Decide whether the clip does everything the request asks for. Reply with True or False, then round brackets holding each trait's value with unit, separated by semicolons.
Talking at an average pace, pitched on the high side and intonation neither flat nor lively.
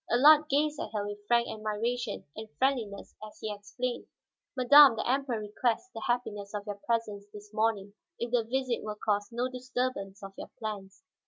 True (175 wpm; 225 Hz; 3.4 semitones)